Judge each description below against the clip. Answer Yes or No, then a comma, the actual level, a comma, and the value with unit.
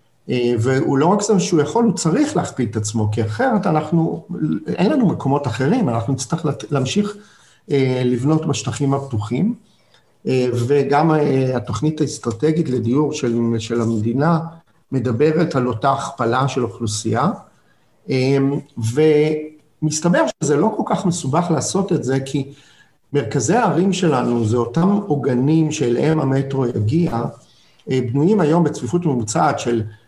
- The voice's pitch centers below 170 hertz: Yes, medium, 140 Hz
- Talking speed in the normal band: Yes, average, 120 wpm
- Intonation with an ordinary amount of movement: Yes, average, 4.5 semitones